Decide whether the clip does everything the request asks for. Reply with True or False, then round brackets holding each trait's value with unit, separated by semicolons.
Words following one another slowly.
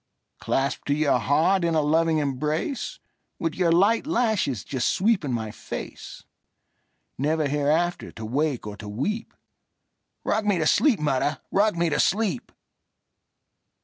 True (120 wpm)